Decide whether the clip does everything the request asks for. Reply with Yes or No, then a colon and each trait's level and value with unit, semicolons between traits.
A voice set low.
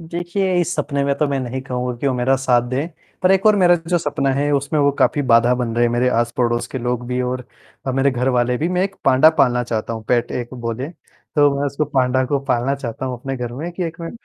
Yes: low, 130 Hz